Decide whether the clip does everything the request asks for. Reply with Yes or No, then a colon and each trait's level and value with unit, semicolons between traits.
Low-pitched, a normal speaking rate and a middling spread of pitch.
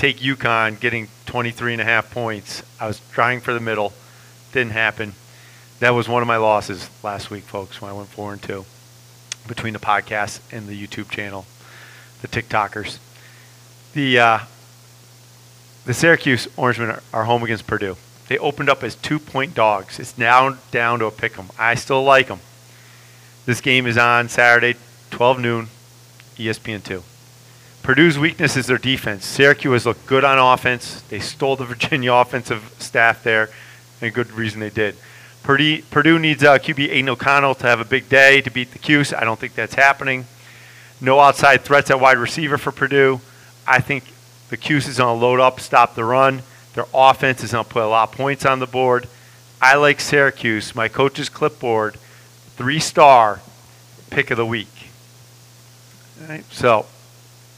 Yes: low, 120 Hz; average, 170 wpm; average, 4.5 semitones